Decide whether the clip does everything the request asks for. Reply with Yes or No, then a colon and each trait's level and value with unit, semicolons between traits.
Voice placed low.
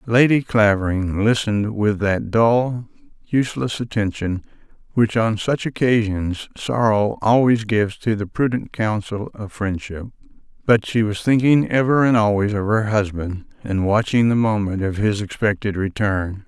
Yes: low, 110 Hz